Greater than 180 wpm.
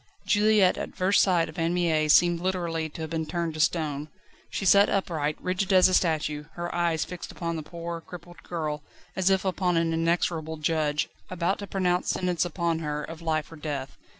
Yes: average, 195 wpm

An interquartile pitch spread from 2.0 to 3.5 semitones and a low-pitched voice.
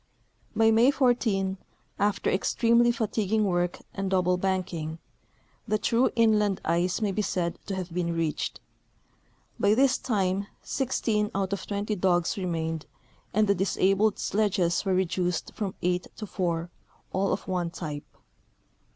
No: average, 3.1 semitones; high, 195 Hz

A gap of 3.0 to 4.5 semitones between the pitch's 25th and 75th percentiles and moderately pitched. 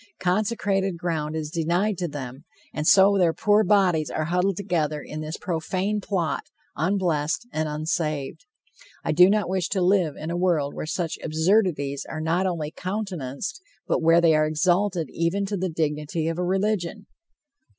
Yes: average, 3.7 semitones; medium, 170 Hz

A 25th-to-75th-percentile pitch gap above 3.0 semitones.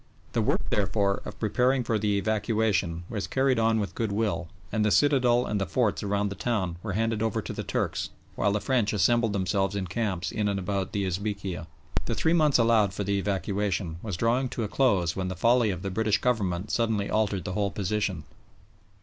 No: average, 2.7 semitones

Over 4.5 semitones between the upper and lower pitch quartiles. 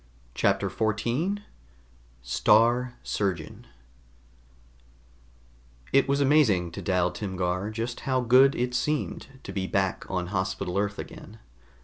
Yes: average, 5.1 semitones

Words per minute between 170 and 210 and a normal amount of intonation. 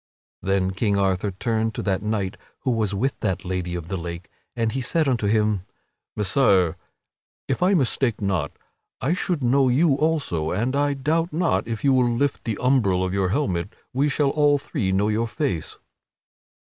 No: average, 180 wpm; wide, 6.3 semitones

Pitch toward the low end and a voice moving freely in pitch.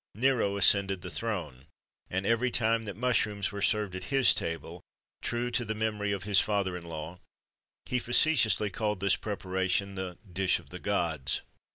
No: low, 100 Hz; average, 3.3 semitones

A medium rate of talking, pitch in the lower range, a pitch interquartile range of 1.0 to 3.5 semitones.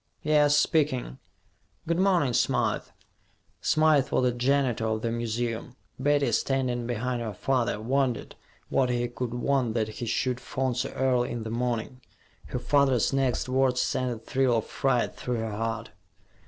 Yes: average, 155 wpm; low, 125 Hz; narrow, 2.4 semitones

